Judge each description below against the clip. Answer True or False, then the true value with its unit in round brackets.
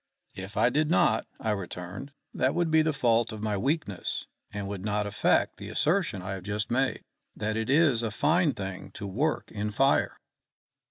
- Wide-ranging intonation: True (5.9 semitones)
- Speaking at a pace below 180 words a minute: False (185 wpm)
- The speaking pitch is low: True (110 Hz)